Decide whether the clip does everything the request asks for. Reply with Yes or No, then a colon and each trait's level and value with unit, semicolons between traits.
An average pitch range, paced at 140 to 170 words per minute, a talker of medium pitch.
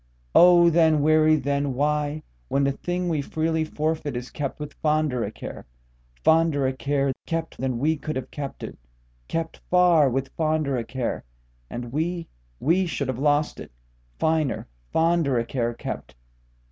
Yes: average, 3.5 semitones; average, 145 wpm; medium, 150 Hz